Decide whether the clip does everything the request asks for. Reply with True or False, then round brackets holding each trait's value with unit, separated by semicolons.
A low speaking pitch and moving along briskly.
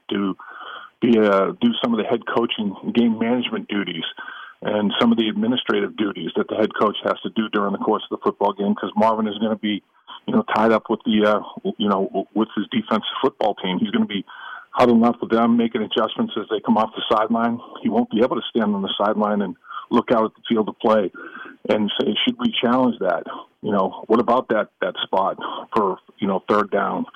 True (115 Hz; 230 wpm)